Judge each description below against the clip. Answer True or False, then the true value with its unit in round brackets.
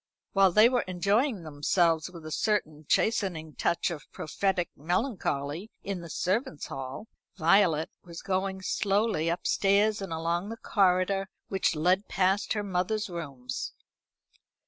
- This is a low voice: False (185 Hz)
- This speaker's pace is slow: True (130 wpm)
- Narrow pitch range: False (3.7 semitones)